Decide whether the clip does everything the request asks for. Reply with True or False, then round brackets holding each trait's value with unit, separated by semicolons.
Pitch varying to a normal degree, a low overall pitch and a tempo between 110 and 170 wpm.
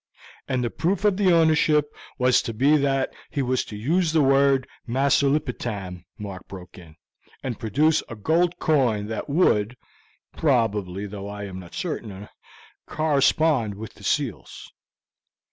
False (6.5 semitones; 130 Hz; 155 wpm)